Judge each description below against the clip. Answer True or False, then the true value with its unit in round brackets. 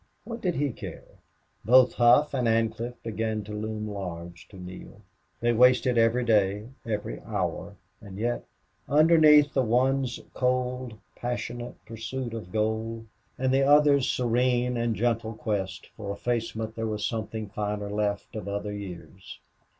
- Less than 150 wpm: True (140 wpm)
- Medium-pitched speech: False (115 Hz)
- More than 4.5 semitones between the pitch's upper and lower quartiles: False (3.0 semitones)